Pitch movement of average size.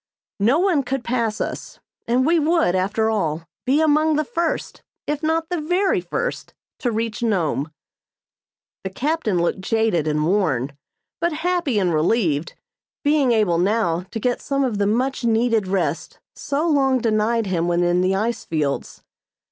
No: wide, 7.8 semitones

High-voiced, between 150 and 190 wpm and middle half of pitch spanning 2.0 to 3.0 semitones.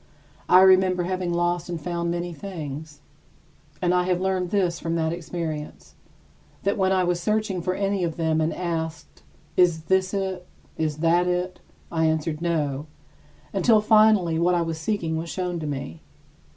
No: medium, 175 Hz; average, 170 wpm; narrow, 2.4 semitones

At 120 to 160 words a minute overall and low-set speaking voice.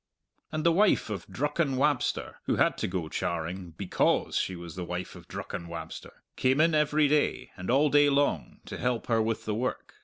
No: average, 195 wpm; low, 125 Hz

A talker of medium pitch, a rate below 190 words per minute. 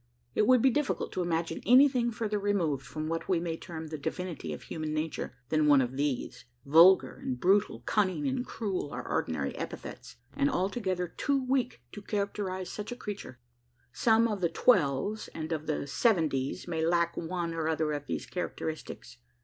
Yes: medium, 175 Hz; average, 175 wpm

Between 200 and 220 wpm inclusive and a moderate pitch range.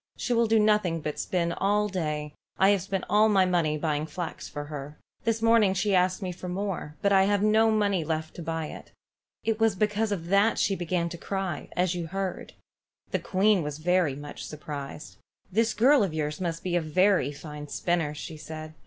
Yes: fast, 205 wpm; average, 4.6 semitones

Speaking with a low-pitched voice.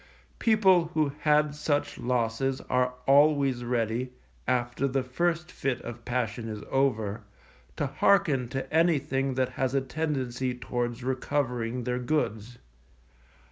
Yes: low, 130 Hz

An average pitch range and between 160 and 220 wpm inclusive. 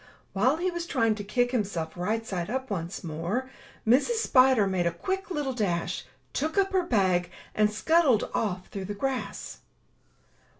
No: wide, 6.3 semitones; average, 165 wpm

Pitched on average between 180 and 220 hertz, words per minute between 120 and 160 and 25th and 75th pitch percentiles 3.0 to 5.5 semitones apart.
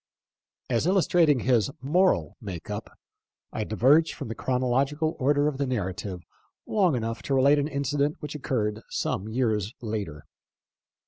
No: low, 130 Hz; average, 140 wpm; average, 5.1 semitones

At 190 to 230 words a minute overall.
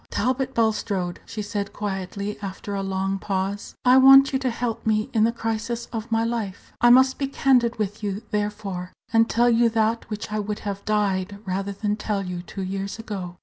Yes: average, 195 wpm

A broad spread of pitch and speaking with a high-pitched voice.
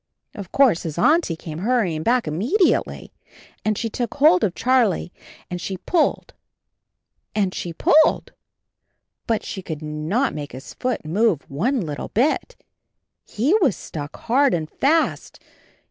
Yes: wide, 8.1 semitones; high, 210 Hz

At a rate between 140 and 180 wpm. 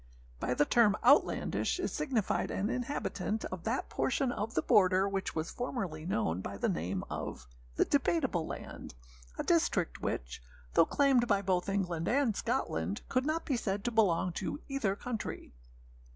Yes: average, 165 wpm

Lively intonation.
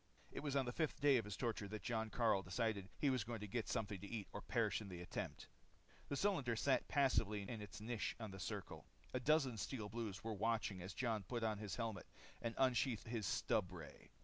No: average, 3.4 semitones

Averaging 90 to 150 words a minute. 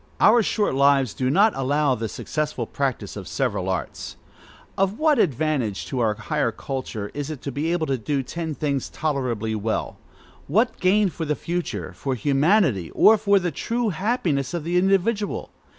No: average, 170 wpm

